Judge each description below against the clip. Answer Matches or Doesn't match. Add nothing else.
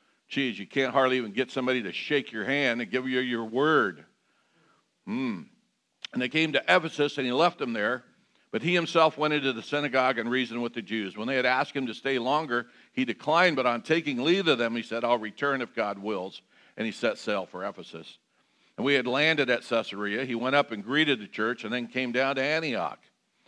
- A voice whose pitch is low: Matches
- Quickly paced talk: Matches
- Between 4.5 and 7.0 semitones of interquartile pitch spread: Doesn't match